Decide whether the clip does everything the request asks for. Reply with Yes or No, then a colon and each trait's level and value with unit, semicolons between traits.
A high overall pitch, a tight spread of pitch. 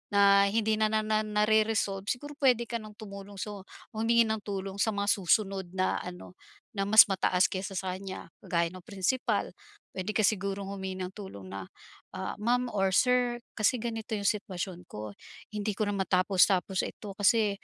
Yes: high, 200 Hz; narrow, 2.3 semitones